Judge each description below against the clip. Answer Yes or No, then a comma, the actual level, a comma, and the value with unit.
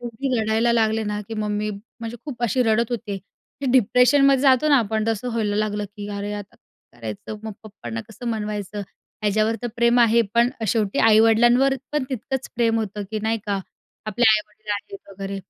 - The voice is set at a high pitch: Yes, high, 220 Hz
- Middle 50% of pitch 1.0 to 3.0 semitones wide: Yes, narrow, 2.4 semitones